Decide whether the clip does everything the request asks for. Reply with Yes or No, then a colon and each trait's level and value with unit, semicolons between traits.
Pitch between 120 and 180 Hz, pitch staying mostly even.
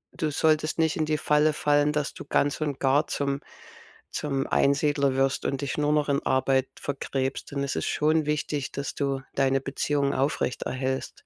Yes: medium, 140 Hz; narrow, 1.8 semitones